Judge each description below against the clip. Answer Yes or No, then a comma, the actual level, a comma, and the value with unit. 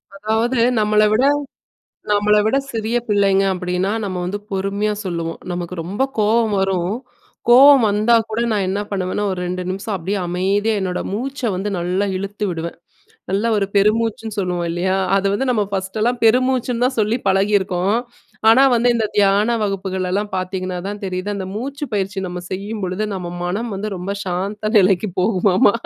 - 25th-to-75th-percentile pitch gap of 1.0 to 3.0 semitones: Yes, average, 2.7 semitones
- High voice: Yes, high, 200 Hz